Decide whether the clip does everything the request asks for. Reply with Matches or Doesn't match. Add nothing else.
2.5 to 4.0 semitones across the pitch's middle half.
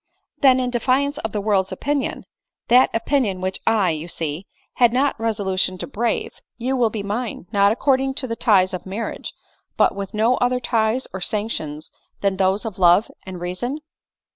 Doesn't match